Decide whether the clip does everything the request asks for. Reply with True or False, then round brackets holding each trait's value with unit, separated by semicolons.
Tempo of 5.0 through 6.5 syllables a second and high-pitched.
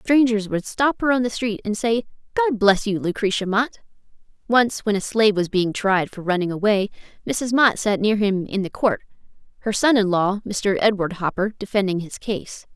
True (5.1 syllables/s; 210 Hz)